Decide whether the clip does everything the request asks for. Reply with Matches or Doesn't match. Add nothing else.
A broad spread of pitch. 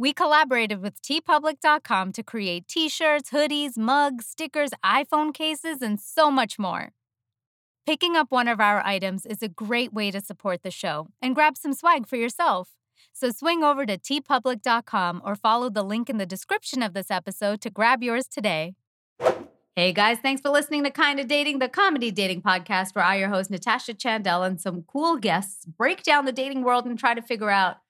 Matches